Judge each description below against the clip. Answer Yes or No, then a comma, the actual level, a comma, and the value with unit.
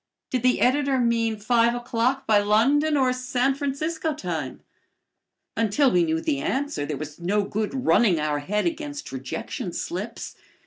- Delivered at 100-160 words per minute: Yes, average, 150 wpm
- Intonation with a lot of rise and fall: Yes, wide, 5.8 semitones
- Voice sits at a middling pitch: No, high, 235 Hz